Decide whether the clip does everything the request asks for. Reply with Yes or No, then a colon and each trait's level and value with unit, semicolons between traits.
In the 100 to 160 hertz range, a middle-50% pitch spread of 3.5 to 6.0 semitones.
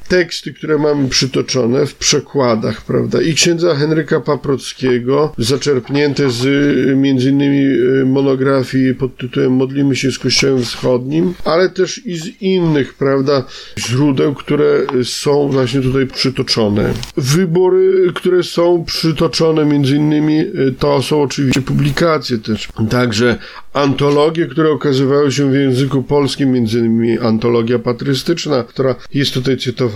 No: medium, 140 Hz; average, 2.8 semitones